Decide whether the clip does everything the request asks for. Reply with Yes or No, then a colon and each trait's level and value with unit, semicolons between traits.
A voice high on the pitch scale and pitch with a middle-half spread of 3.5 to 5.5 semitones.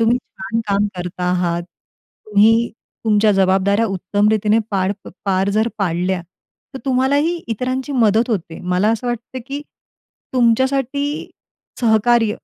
Yes: high, 220 Hz; average, 3.9 semitones